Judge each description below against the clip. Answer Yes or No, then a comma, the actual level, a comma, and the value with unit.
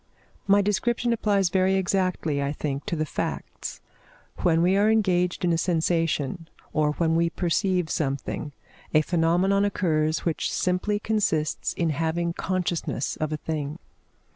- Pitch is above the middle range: No, medium, 170 Hz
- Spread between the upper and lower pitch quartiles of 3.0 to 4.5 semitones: Yes, average, 3.5 semitones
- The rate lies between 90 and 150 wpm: Yes, average, 140 wpm